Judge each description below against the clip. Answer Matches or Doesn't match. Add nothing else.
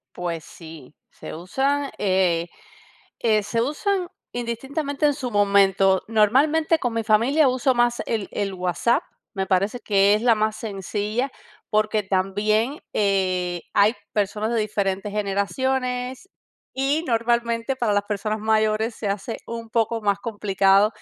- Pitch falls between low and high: Doesn't match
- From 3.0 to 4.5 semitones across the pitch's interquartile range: Matches